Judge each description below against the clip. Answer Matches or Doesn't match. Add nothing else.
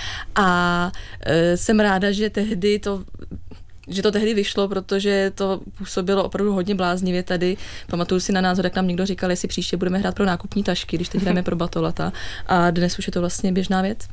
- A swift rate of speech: Matches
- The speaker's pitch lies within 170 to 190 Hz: Matches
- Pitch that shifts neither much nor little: Doesn't match